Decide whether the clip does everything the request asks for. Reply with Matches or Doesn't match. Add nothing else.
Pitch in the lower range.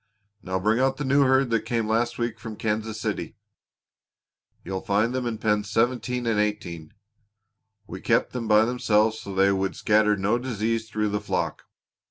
Matches